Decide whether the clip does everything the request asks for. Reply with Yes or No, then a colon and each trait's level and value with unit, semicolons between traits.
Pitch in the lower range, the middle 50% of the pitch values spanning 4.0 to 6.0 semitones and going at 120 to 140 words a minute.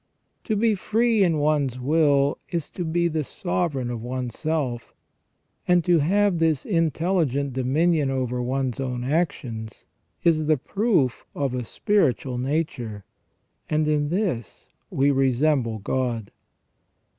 No: medium, 145 Hz; average, 4.7 semitones; slow, 135 wpm